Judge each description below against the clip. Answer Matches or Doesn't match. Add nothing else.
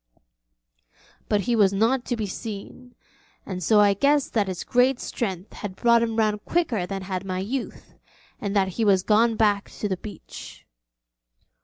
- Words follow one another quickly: Doesn't match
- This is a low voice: Doesn't match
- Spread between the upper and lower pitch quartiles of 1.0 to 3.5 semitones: Matches